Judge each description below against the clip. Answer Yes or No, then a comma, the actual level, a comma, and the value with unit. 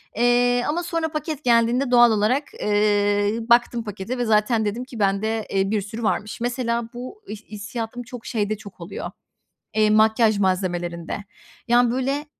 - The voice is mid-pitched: No, high, 225 Hz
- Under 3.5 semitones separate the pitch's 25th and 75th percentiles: Yes, average, 2.9 semitones